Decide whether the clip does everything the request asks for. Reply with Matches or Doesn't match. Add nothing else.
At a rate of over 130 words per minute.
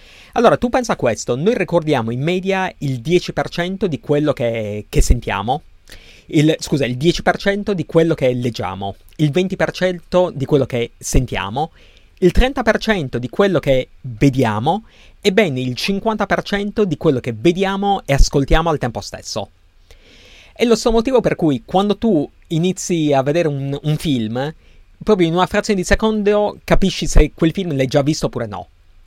Matches